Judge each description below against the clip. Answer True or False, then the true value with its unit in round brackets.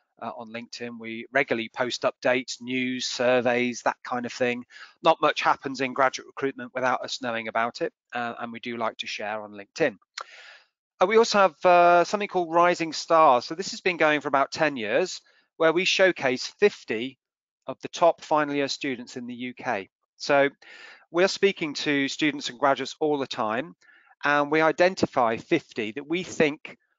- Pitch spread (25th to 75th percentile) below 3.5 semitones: False (5.2 semitones)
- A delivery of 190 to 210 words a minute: False (180 wpm)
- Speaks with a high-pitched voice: False (140 Hz)